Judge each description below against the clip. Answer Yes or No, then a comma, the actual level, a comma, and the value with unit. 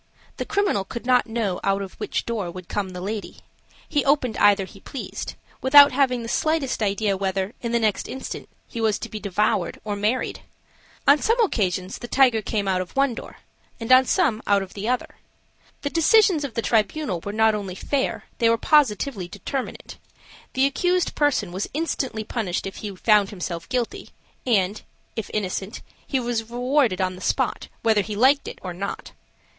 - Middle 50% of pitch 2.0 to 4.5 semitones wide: No, average, 4.9 semitones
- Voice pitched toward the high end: Yes, high, 220 Hz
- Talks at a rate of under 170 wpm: No, average, 185 wpm